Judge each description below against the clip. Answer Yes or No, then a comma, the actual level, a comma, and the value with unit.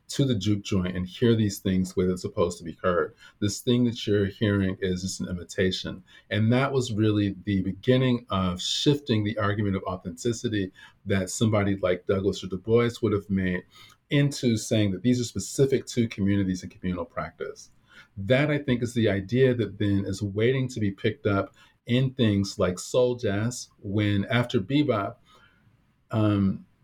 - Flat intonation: No, average, 3.8 semitones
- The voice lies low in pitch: Yes, low, 105 Hz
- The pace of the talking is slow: No, average, 175 wpm